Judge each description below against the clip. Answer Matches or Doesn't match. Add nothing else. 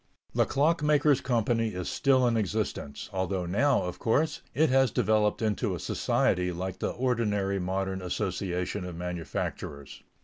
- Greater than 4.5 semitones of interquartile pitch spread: Matches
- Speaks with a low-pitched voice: Matches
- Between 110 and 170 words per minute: Matches